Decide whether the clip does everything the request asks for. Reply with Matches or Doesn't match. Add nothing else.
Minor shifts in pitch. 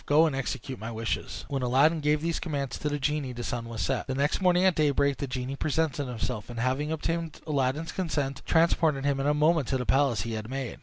Doesn't match